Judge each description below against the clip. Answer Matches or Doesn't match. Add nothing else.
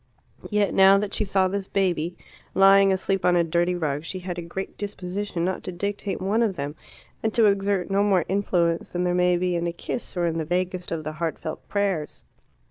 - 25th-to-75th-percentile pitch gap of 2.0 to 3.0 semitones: Matches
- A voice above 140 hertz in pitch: Matches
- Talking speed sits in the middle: Doesn't match